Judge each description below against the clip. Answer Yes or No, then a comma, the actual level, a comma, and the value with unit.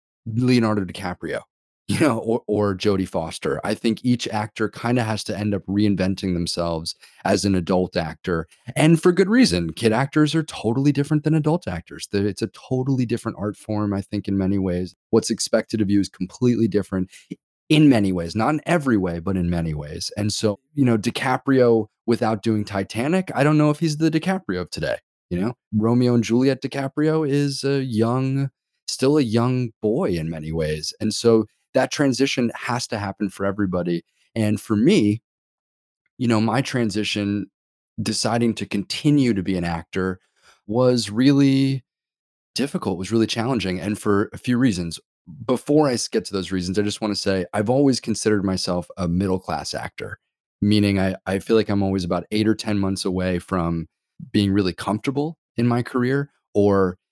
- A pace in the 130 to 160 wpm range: No, average, 180 wpm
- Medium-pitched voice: No, low, 110 Hz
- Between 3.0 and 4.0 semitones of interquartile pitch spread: No, average, 4.7 semitones